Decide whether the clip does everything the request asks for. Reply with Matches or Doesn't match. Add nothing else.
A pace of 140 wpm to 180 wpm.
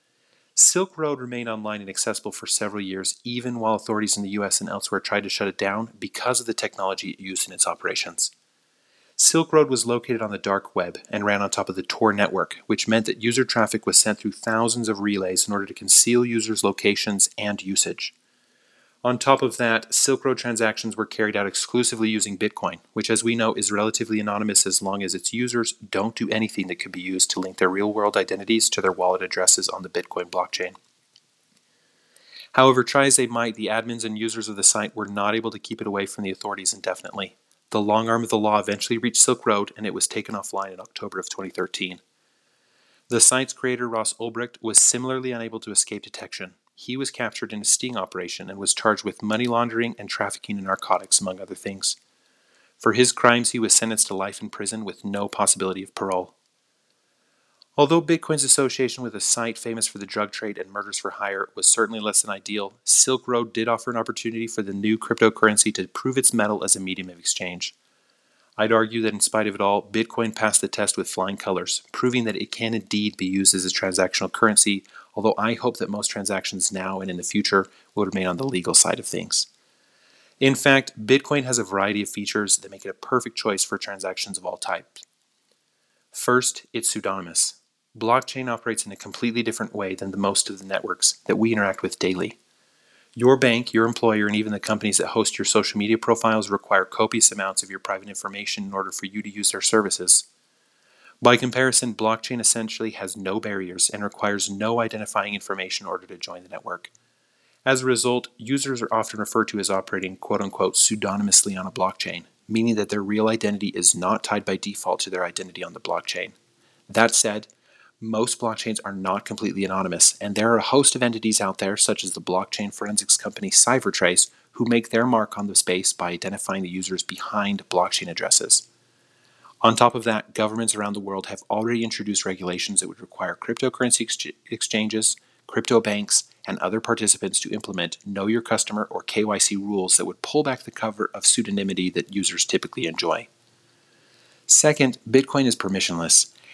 Doesn't match